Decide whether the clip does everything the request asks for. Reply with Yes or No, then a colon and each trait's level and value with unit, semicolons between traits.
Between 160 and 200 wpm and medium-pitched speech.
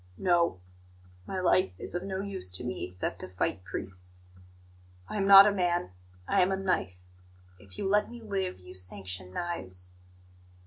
Yes: average, 170 wpm; medium, 170 Hz